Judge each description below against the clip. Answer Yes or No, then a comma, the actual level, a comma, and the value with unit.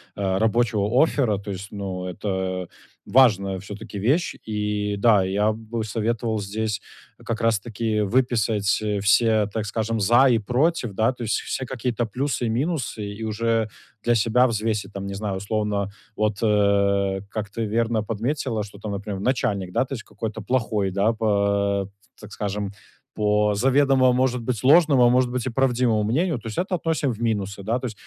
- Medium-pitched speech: No, low, 110 Hz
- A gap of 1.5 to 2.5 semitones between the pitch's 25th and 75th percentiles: No, average, 2.9 semitones